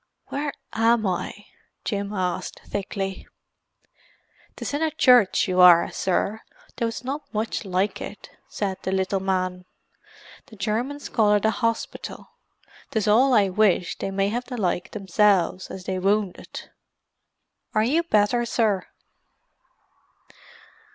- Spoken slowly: Yes, slow, 130 wpm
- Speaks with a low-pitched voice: No, high, 205 Hz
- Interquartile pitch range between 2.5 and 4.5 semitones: Yes, average, 3.3 semitones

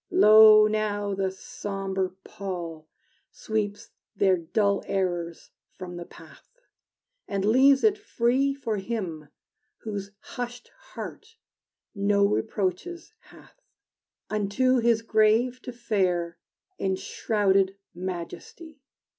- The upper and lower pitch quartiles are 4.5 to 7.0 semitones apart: No, average, 3.7 semitones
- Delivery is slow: Yes, slow, 100 wpm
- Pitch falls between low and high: No, high, 205 Hz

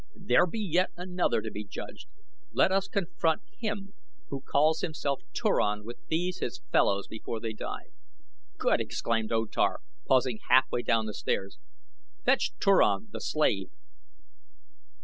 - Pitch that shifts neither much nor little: No, wide, 8.5 semitones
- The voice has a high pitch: No, medium, 140 Hz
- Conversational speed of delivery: Yes, average, 145 wpm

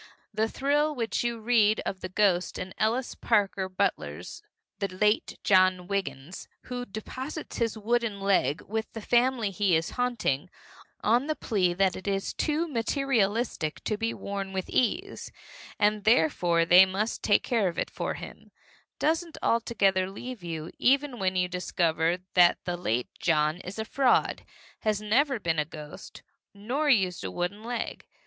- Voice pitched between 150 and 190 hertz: No, high, 205 Hz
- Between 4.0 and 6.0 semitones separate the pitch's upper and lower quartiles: Yes, average, 4.7 semitones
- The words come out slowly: No, average, 160 wpm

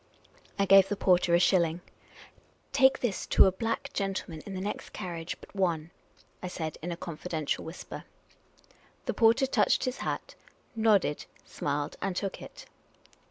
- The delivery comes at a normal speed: Yes, average, 160 wpm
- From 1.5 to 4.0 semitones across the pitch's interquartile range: Yes, average, 3.5 semitones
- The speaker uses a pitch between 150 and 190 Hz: Yes, medium, 185 Hz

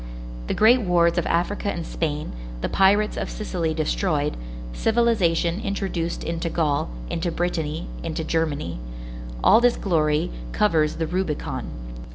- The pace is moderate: No, slow, 125 wpm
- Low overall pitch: No, medium, 165 Hz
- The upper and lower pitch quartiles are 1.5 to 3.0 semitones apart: No, average, 3.9 semitones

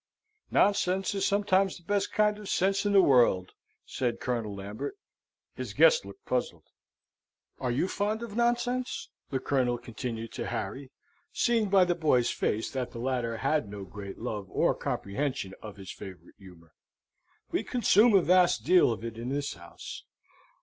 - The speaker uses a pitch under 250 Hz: Yes, low, 135 Hz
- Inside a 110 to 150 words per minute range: No, average, 165 wpm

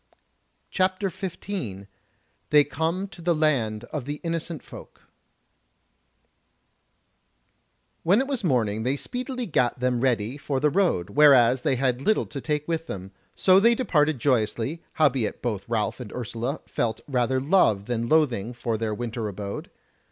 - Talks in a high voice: No, low, 135 Hz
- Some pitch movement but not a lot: No, wide, 6.1 semitones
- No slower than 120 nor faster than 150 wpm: Yes, average, 145 wpm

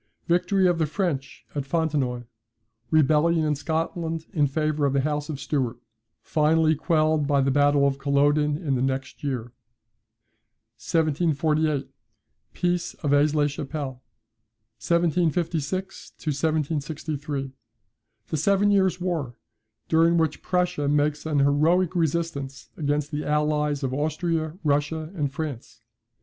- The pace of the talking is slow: Yes, slow, 125 wpm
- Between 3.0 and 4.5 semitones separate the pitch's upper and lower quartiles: No, narrow, 2.4 semitones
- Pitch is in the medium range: Yes, medium, 150 Hz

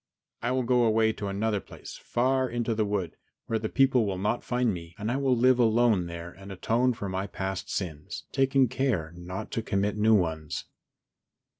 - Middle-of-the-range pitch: No, low, 110 Hz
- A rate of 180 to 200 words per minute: Yes, average, 190 wpm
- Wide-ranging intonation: No, average, 4.3 semitones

